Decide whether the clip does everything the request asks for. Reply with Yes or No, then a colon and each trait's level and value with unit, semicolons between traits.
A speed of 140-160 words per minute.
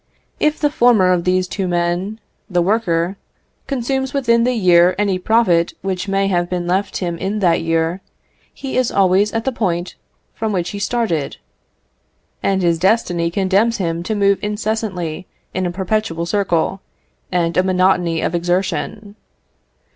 Yes: average, 155 wpm